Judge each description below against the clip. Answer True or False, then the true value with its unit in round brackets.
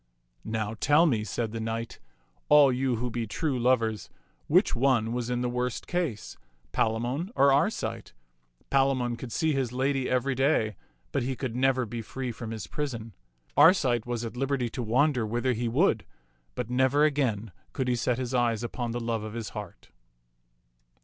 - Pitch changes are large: False (2.7 semitones)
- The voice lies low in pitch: True (125 Hz)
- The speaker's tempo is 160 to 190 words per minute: True (175 wpm)